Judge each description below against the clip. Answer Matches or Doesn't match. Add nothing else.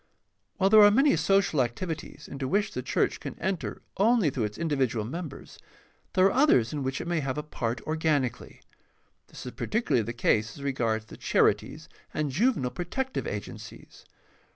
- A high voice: Doesn't match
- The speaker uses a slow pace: Doesn't match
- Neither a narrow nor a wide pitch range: Doesn't match